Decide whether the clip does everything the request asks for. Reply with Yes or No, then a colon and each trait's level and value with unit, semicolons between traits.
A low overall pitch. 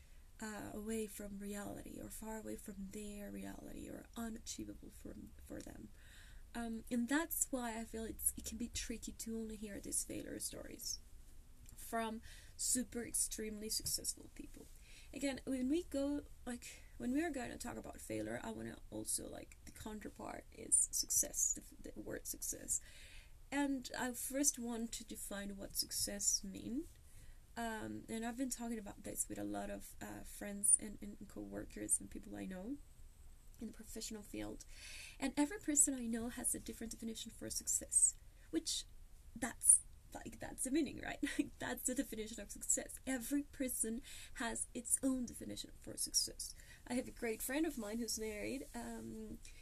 No: high, 225 Hz